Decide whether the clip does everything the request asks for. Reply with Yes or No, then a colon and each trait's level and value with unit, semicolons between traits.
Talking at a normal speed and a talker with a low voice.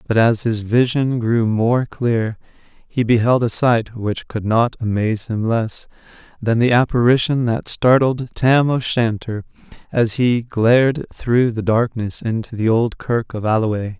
Yes: average, 160 wpm; low, 115 Hz